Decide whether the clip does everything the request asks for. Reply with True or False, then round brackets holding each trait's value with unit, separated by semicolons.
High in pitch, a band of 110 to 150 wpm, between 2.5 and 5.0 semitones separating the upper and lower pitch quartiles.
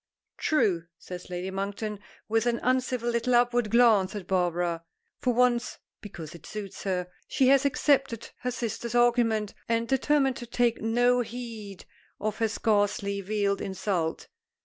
True (225 Hz; 145 wpm; 3.6 semitones)